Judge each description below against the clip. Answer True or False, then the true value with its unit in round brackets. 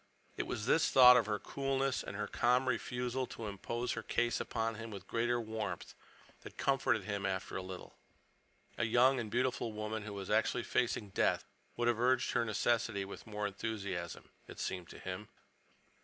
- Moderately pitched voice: False (110 Hz)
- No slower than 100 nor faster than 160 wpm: False (180 wpm)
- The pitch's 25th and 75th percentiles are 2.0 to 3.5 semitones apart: True (3.1 semitones)